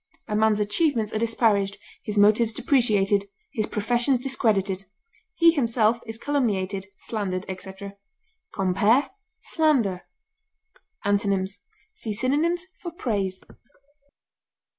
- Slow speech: Yes, slow, 95 wpm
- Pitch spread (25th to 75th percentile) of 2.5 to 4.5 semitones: Yes, average, 4.0 semitones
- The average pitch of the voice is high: Yes, high, 215 Hz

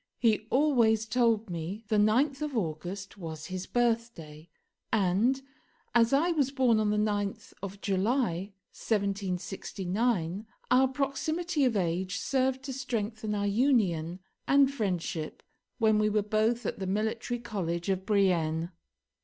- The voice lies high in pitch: Yes, high, 215 Hz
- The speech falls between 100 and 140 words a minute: Yes, slow, 135 wpm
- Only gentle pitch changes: No, average, 4.5 semitones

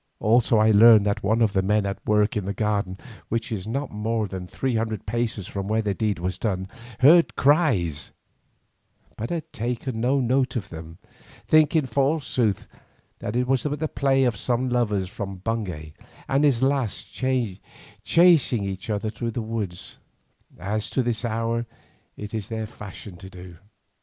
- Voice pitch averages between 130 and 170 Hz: No, low, 110 Hz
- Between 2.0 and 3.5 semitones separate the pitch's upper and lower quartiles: No, average, 3.9 semitones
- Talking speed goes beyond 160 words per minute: Yes, average, 170 wpm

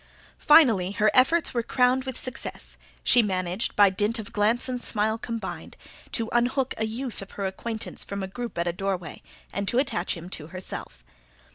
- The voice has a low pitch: No, high, 220 Hz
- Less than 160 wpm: No, average, 180 wpm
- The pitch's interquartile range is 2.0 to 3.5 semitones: No, average, 4.3 semitones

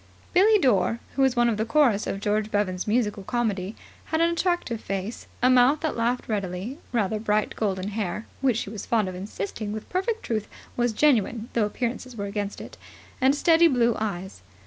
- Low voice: No, high, 225 Hz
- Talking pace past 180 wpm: Yes, average, 190 wpm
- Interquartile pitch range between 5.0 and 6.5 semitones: No, average, 3.8 semitones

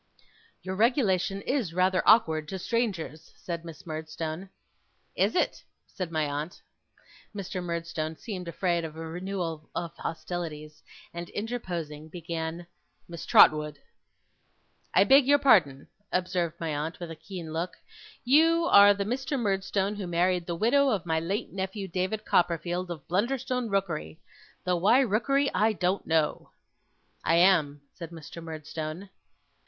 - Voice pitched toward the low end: No, medium, 180 Hz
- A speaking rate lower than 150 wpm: Yes, average, 140 wpm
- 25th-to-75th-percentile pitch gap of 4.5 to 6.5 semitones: No, average, 3.7 semitones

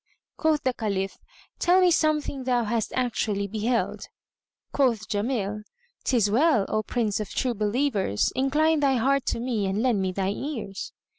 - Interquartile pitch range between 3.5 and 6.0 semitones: Yes, average, 4.8 semitones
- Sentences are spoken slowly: No, average, 155 wpm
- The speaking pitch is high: Yes, high, 235 Hz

